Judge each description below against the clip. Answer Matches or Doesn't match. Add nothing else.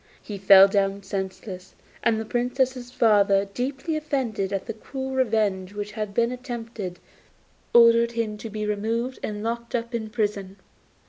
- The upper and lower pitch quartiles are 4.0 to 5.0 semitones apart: Doesn't match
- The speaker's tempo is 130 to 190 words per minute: Matches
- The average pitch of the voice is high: Matches